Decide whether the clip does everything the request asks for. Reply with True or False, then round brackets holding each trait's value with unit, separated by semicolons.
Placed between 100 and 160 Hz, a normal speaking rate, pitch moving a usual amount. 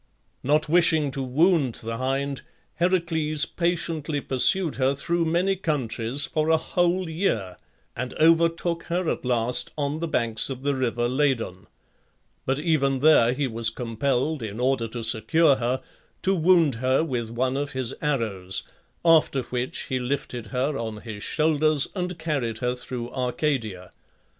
True (135 Hz; 150 wpm; 4.7 semitones)